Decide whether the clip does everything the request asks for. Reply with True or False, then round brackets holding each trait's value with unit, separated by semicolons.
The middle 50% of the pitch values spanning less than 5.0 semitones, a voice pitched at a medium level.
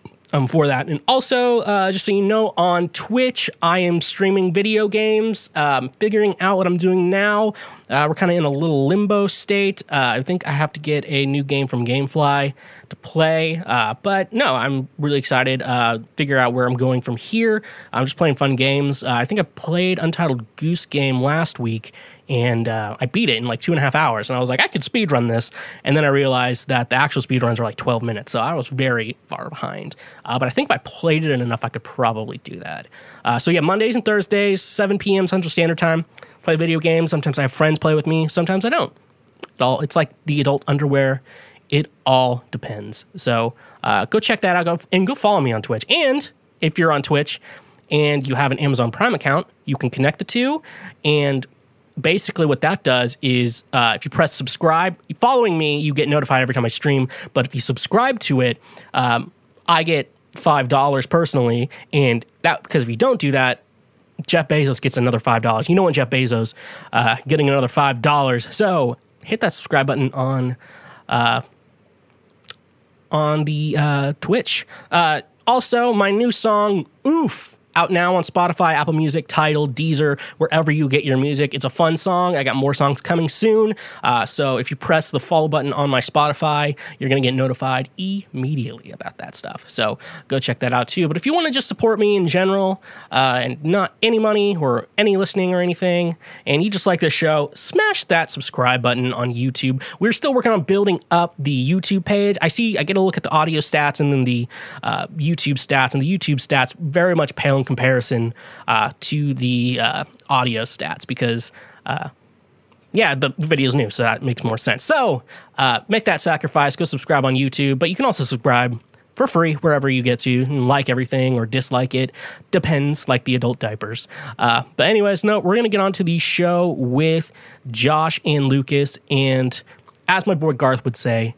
False (5.4 semitones; 150 Hz)